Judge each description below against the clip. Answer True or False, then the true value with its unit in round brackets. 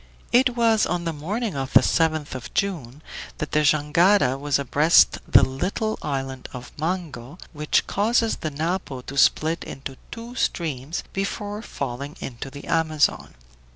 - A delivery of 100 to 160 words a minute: True (150 wpm)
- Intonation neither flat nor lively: False (5.9 semitones)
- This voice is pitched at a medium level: True (155 Hz)